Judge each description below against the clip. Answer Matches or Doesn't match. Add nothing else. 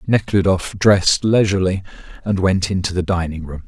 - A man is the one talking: Matches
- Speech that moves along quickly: Doesn't match